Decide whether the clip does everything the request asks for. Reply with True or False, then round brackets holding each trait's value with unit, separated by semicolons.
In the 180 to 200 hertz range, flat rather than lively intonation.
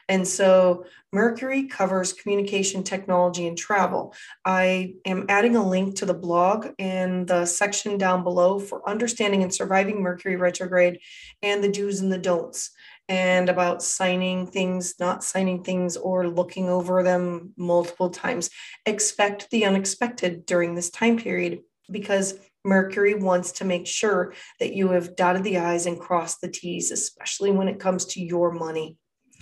True (185 Hz; 1.7 semitones)